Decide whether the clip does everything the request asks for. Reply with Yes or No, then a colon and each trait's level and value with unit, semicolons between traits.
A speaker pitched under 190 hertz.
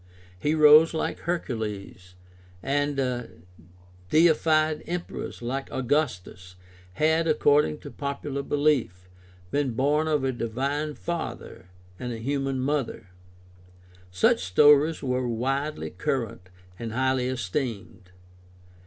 Yes: low, 135 Hz